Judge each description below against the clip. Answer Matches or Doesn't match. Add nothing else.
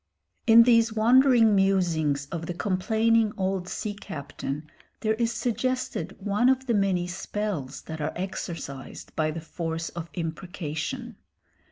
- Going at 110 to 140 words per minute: Matches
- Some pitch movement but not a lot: Doesn't match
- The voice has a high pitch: Matches